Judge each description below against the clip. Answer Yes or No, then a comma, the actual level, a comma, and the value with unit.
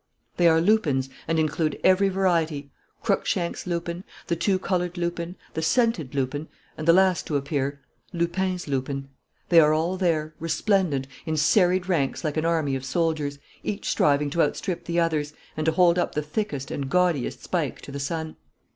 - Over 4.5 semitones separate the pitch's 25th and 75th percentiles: No, average, 3.4 semitones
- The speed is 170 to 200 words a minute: Yes, average, 175 wpm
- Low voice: No, medium, 165 Hz